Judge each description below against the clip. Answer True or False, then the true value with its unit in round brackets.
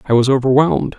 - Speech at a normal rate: True (185 wpm)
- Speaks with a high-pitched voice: False (125 Hz)